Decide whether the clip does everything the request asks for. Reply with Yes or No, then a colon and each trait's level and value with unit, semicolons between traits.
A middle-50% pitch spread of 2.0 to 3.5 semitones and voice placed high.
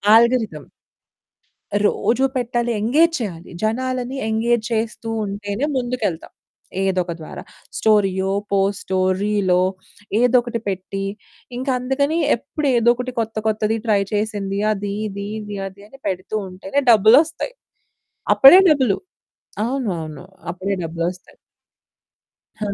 No: average, 3.9 semitones; high, 215 Hz